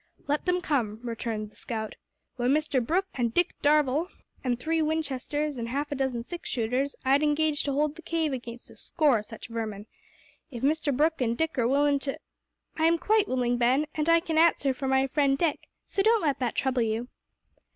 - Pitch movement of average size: Yes, average, 4.4 semitones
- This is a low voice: No, very high, 280 Hz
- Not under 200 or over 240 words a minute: Yes, fast, 205 wpm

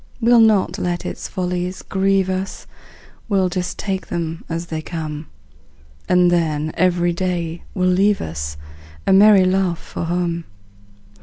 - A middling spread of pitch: No, narrow, 2.2 semitones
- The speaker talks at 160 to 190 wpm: No, average, 140 wpm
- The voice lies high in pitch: No, medium, 180 Hz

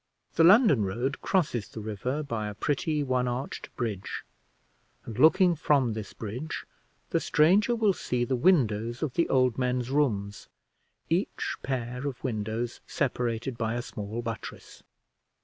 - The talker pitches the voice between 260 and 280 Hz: No, low, 125 Hz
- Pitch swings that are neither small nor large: Yes, average, 4.6 semitones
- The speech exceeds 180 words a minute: No, average, 145 wpm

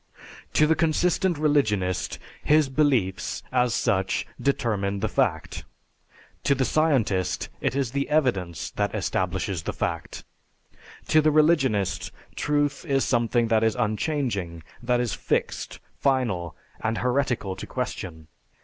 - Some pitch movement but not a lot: No, wide, 6.3 semitones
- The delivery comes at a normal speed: No, slow, 125 wpm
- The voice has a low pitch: Yes, low, 125 Hz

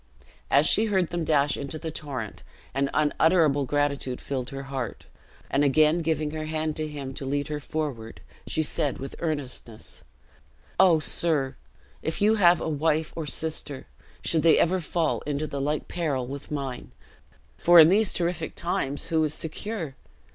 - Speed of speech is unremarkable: Yes, average, 165 wpm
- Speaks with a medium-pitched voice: Yes, medium, 155 Hz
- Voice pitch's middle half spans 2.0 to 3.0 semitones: Yes, average, 2.7 semitones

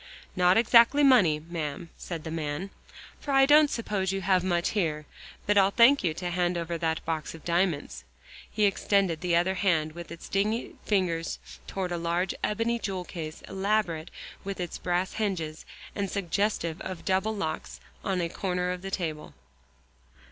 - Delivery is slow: No, average, 170 wpm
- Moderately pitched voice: Yes, medium, 180 Hz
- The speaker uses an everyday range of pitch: Yes, average, 3.1 semitones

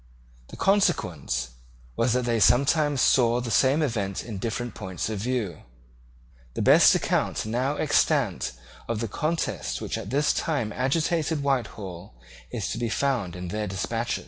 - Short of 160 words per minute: Yes, average, 150 wpm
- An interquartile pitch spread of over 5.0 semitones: Yes, wide, 5.6 semitones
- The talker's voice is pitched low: Yes, low, 120 Hz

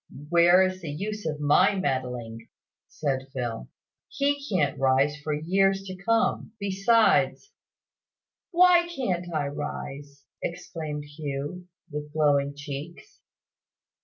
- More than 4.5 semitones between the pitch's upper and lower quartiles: Yes, wide, 5.4 semitones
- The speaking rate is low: Yes, slow, 115 wpm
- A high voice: No, medium, 155 Hz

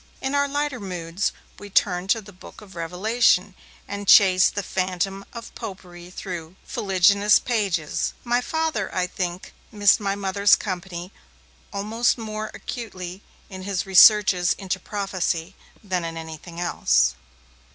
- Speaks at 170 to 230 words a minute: No, average, 140 wpm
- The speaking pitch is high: Yes, high, 195 Hz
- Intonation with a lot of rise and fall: No, average, 2.8 semitones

